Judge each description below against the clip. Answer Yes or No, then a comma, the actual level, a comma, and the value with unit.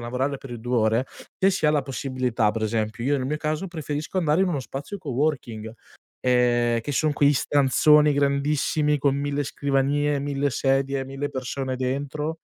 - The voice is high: No, medium, 140 Hz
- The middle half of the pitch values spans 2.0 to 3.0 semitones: Yes, narrow, 2.6 semitones